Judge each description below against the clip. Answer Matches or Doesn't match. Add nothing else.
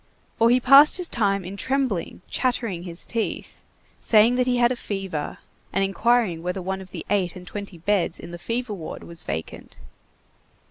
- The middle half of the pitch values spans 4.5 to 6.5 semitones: Matches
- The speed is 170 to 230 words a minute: Matches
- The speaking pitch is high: Matches